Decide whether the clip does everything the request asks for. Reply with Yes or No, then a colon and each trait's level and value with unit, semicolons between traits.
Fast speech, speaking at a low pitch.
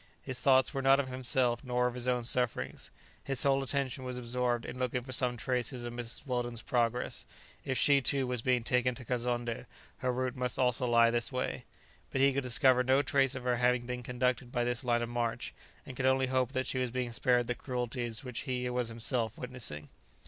Yes: fast, 215 wpm; low, 125 Hz